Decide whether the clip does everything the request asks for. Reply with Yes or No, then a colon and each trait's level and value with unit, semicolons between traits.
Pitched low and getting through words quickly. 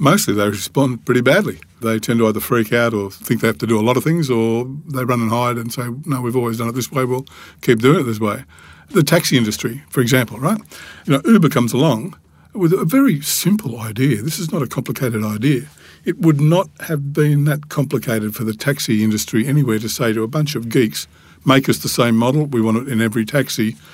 Yes: low, 125 Hz; fast, 235 wpm